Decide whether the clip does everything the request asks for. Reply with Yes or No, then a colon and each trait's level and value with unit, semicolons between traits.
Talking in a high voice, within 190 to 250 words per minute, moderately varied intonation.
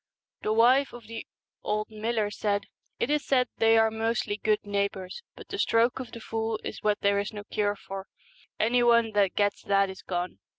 No: high, 215 Hz; average, 200 wpm; narrow, 2.1 semitones